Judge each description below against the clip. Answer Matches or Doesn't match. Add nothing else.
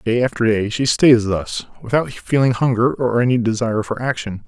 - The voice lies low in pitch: Matches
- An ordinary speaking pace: Matches